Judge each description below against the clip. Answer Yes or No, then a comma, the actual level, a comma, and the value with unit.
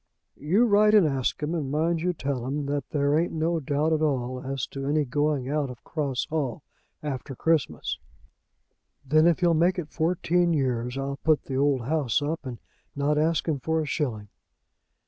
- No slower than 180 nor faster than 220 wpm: Yes, average, 185 wpm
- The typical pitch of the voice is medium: Yes, medium, 150 Hz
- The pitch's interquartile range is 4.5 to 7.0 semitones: No, average, 3.0 semitones